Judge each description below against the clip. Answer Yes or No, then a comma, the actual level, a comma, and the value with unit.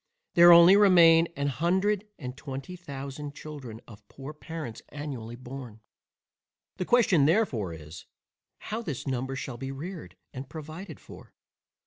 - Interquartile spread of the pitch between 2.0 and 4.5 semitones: No, average, 5.0 semitones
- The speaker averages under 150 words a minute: Yes, slow, 135 wpm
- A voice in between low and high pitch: Yes, medium, 145 Hz